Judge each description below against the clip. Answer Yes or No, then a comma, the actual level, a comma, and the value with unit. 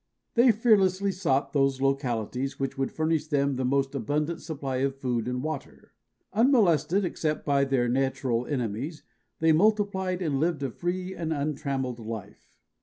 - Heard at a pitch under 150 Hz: Yes, medium, 140 Hz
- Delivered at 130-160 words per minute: Yes, average, 150 wpm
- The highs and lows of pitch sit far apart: No, average, 4.7 semitones